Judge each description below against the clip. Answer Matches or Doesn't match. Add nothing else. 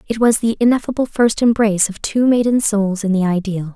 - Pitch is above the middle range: Matches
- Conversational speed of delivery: Doesn't match